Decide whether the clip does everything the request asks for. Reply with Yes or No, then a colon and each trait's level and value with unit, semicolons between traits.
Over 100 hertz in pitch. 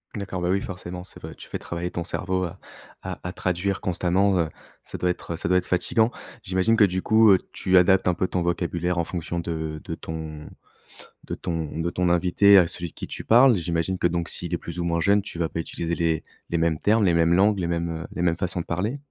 No: very low, 90 Hz